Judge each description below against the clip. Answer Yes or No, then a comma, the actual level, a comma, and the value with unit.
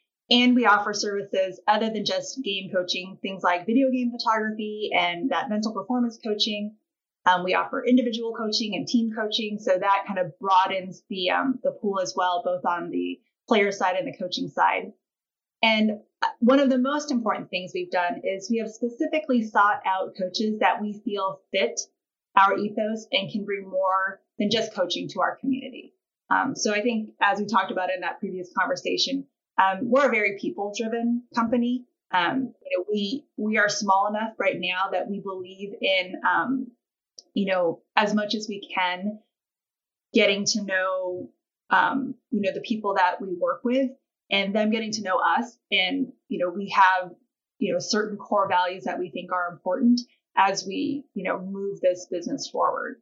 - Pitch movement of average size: Yes, average, 4.1 semitones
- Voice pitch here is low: No, high, 210 Hz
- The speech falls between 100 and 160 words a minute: No, average, 180 wpm